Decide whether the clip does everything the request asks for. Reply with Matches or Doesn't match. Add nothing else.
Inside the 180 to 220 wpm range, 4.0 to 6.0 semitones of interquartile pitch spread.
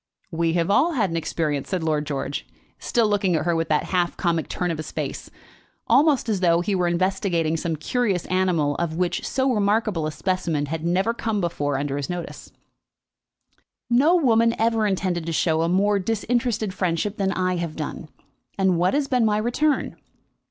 Matches